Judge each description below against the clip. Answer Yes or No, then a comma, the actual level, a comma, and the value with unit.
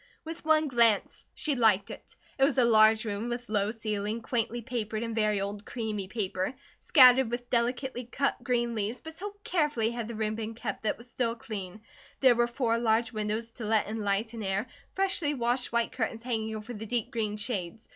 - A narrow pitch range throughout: Yes, narrow, 2.2 semitones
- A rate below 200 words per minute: No, fast, 205 wpm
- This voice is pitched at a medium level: No, high, 230 Hz